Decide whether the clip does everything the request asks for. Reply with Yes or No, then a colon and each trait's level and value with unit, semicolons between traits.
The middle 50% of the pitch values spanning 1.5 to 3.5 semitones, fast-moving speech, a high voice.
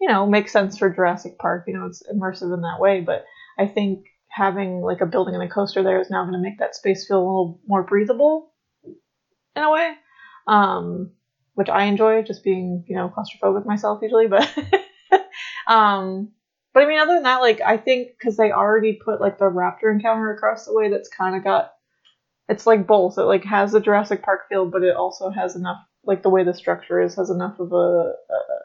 Yes: average, 3.2 semitones; fast, 215 wpm; high, 200 Hz